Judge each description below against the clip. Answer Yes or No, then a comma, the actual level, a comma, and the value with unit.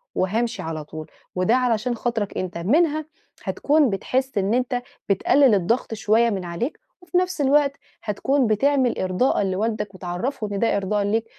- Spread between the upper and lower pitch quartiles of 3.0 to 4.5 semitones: No, average, 5.2 semitones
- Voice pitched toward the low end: No, high, 225 Hz